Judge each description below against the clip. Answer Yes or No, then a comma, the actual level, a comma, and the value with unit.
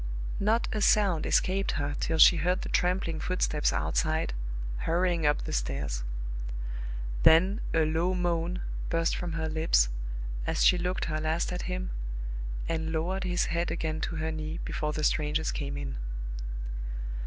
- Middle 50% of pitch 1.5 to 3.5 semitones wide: Yes, narrow, 2.4 semitones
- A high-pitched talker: No, medium, 165 Hz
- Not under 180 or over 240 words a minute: No, average, 155 wpm